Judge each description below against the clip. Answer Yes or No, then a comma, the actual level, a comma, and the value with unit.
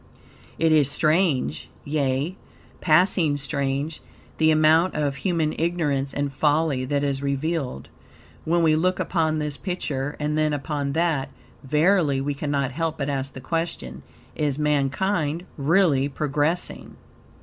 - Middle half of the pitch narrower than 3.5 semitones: Yes, average, 2.7 semitones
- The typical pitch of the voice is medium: Yes, medium, 150 Hz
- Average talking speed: No, slow, 130 wpm